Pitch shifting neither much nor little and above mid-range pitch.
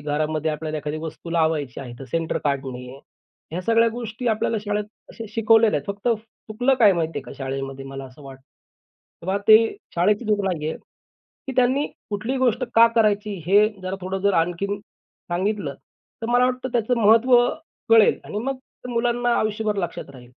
No: wide, 6.5 semitones; high, 200 Hz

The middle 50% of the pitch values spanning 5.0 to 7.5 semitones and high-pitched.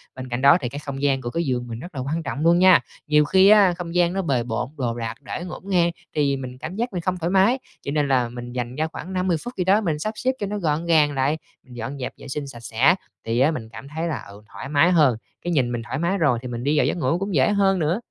No: wide, 5.6 semitones; medium, 150 Hz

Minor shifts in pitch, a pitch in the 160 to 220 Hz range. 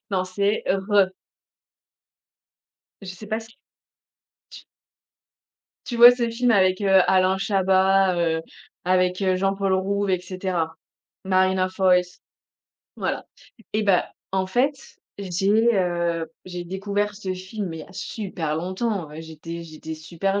Yes: narrow, 1.9 semitones; high, 190 Hz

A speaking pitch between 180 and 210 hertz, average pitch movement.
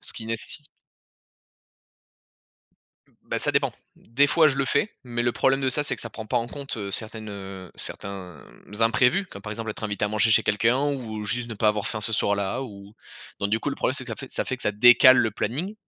No: low, 115 Hz; average, 3.6 semitones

